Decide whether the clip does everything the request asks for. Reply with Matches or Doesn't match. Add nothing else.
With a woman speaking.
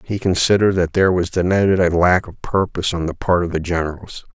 Doesn't match